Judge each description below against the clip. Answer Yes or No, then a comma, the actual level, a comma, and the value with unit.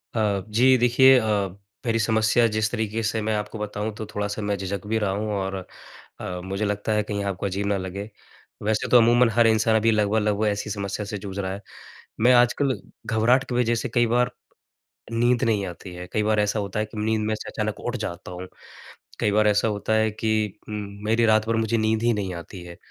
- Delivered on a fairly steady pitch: Yes, narrow, 1.9 semitones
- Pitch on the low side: Yes, low, 110 Hz